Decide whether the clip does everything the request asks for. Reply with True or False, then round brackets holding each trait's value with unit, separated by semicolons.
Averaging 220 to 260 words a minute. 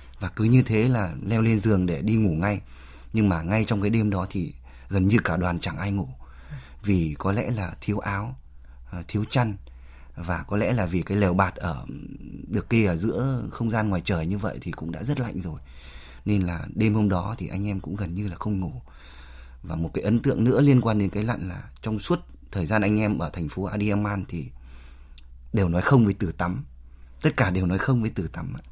True (230 wpm)